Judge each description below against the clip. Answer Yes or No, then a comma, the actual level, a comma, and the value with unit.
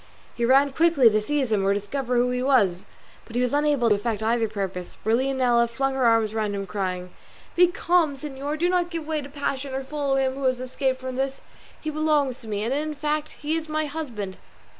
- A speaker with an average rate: No, fast, 225 wpm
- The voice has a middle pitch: No, very high, 265 Hz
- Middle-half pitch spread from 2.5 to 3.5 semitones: No, average, 4.6 semitones